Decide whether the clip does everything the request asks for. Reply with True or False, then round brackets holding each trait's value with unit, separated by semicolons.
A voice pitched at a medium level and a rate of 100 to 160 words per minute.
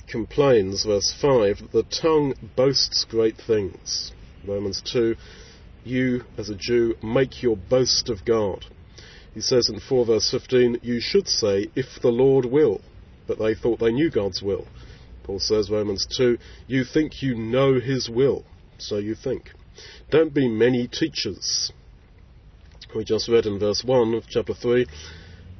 False (115 Hz; 155 wpm)